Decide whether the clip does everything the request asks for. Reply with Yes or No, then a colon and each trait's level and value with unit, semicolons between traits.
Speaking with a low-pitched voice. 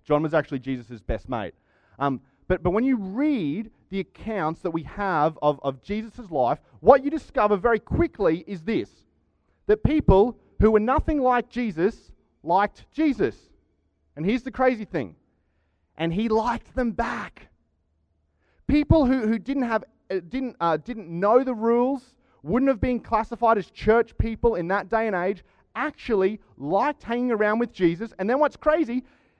No: high, 215 Hz